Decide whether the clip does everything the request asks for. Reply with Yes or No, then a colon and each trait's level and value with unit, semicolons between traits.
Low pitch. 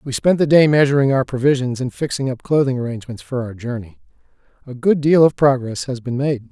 Yes: low, 130 Hz